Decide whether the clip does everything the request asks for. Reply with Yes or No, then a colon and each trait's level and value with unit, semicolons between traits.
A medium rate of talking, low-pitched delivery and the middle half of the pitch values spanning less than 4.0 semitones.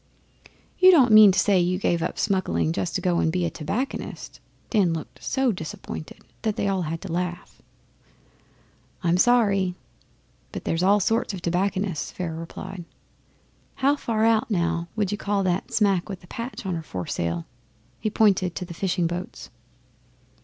No: average, 165 wpm; medium, 185 Hz; average, 3.5 semitones